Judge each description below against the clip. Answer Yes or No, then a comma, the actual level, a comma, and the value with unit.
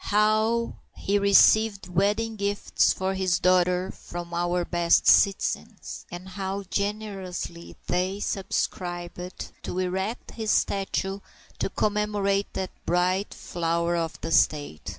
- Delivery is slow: Yes, slow, 115 wpm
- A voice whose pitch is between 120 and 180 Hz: No, high, 190 Hz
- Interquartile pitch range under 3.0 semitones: Yes, narrow, 2.5 semitones